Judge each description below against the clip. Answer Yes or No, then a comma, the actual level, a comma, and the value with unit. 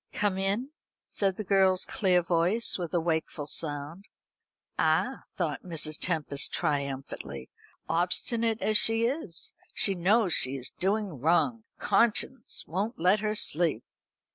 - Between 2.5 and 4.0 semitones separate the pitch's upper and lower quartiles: No, average, 4.8 semitones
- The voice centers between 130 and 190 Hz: Yes, medium, 185 Hz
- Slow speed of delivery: Yes, slow, 130 wpm